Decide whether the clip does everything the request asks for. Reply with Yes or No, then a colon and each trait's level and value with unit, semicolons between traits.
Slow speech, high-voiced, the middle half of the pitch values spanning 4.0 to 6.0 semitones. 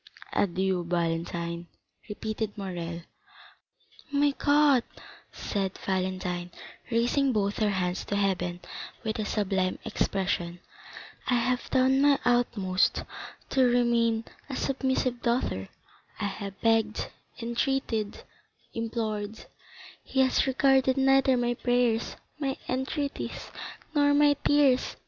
Yes: slow, 105 wpm; high, 230 Hz; wide, 5.5 semitones